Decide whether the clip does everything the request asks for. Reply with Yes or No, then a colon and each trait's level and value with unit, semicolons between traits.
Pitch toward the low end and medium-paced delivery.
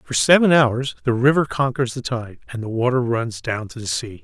No: low, 125 Hz; fast, 210 wpm